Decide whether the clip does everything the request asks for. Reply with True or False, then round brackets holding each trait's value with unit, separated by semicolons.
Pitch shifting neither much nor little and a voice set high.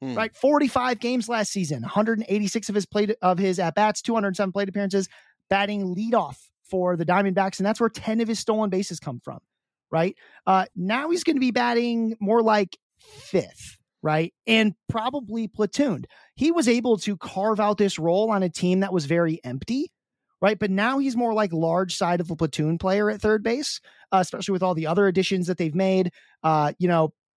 True (3.8 semitones; 200 Hz)